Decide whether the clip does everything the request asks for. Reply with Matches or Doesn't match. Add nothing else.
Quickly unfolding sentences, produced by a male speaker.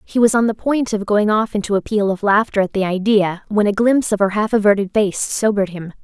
Doesn't match